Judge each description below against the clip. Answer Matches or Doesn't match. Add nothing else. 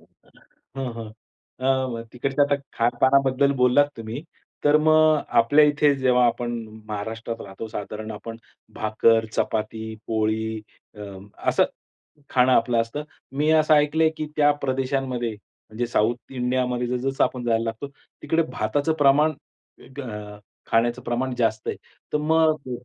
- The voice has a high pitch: Doesn't match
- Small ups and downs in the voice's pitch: Doesn't match